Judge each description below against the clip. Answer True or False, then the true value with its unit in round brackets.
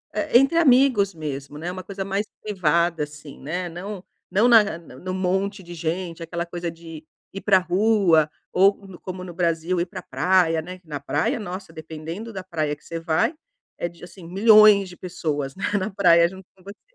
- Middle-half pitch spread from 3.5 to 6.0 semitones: False (3.1 semitones)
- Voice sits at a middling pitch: True (180 Hz)